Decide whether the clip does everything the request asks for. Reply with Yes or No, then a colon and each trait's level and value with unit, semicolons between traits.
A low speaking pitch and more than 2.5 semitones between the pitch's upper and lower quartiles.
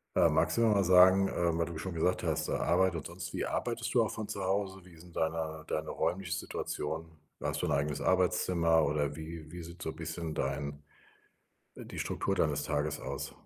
Yes: very low, 85 Hz; average, 2.9 semitones